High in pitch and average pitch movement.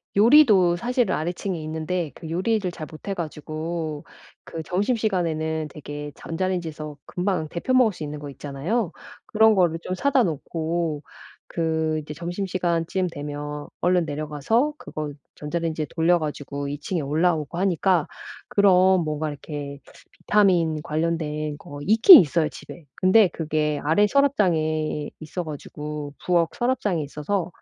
No: medium, 165 Hz; average, 3.5 semitones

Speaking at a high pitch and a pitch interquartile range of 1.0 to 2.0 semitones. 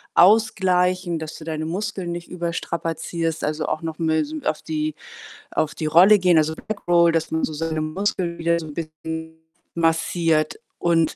No: medium, 165 Hz; narrow, 1.7 semitones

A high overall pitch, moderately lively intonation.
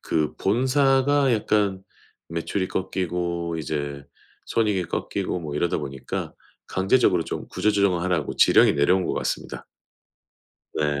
No: very low, 90 Hz; average, 4.7 semitones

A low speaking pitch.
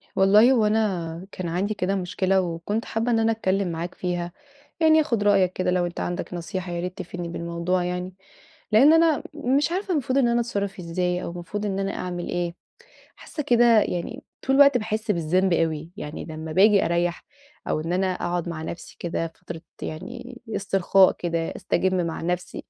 No: medium, 185 Hz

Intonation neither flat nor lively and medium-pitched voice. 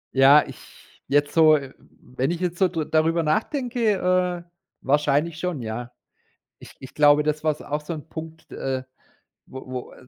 Yes: average, 3.1 semitones; medium, 155 Hz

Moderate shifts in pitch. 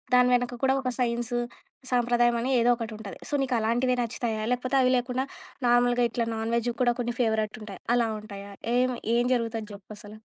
No: narrow, 1.8 semitones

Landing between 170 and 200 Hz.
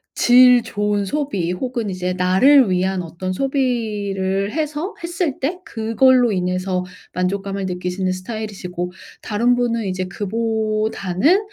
No: high, 210 Hz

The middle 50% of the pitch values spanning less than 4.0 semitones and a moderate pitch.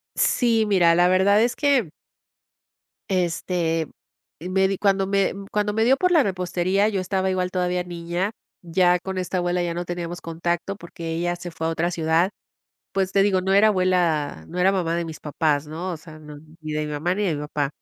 Yes: narrow, 2.6 semitones; medium, 180 Hz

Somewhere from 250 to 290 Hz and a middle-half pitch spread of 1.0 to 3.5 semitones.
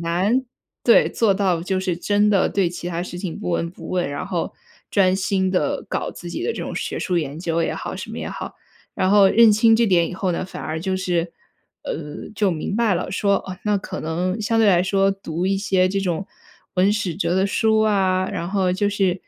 No: high, 190 Hz; narrow, 2.4 semitones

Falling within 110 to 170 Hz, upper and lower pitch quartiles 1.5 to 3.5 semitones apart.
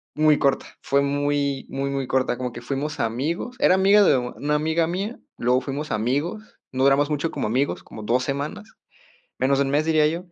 Yes: medium, 140 Hz; average, 2.9 semitones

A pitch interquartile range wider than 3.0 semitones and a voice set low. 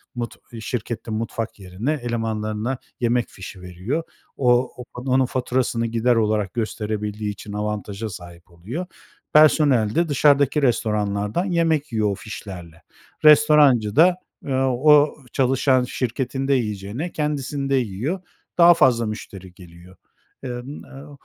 Yes: average, 4.7 semitones; low, 120 Hz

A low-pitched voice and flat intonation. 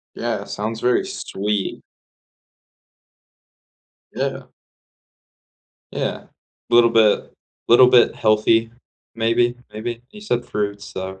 Yes: low, 115 Hz; narrow, 2.3 semitones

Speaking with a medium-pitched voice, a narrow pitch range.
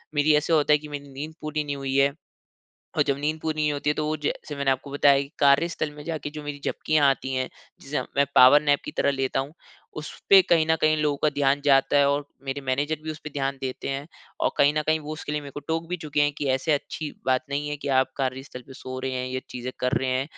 Yes: medium, 145 Hz; narrow, 2.0 semitones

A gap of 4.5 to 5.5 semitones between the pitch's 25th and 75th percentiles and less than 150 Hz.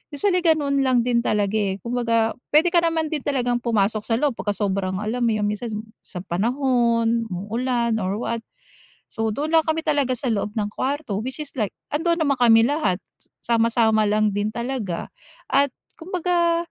No: average, 5.1 semitones; high, 235 Hz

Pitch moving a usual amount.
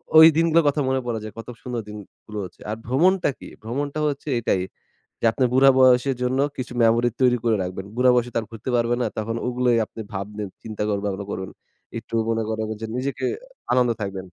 Yes: average, 3.2 semitones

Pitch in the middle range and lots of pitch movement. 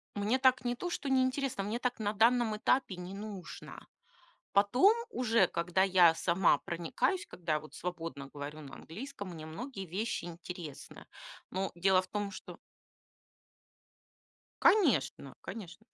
No: high, 195 Hz; wide, 6.1 semitones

